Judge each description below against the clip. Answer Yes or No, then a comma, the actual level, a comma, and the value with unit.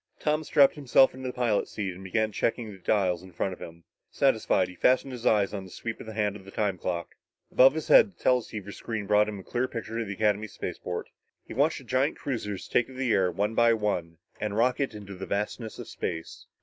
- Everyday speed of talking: No, fast, 225 wpm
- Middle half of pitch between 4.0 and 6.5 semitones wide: Yes, average, 4.3 semitones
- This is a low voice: Yes, low, 110 Hz